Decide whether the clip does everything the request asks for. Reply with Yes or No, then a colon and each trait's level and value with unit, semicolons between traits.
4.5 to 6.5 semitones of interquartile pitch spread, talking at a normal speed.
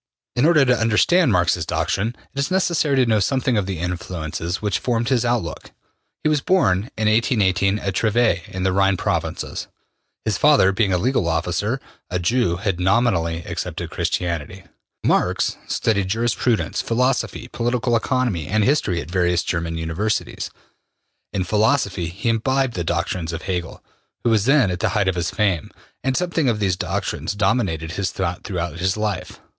Yes: average, 5.3 semitones; average, 170 wpm